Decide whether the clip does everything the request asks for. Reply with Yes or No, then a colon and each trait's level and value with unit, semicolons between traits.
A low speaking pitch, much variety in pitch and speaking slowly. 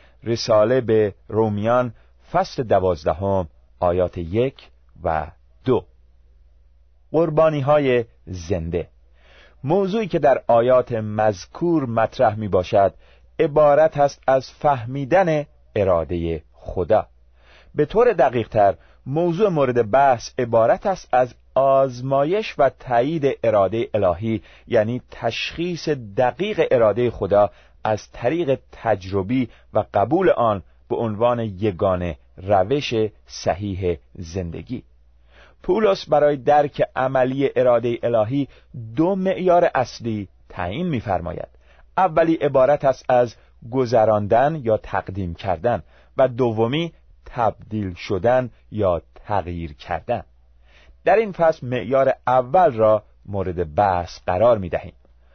Yes: low, 115 Hz; wide, 7.6 semitones; slow, 100 wpm